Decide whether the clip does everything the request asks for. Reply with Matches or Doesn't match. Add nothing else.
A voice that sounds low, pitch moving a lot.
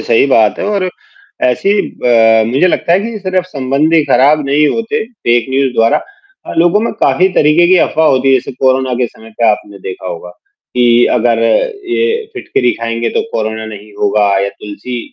Matches